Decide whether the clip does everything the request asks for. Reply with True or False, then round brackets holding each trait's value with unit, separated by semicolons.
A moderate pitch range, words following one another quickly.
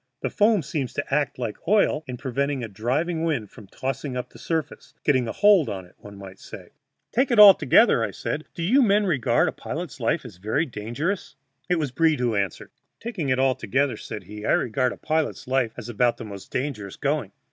False (6.3 semitones; 210 wpm)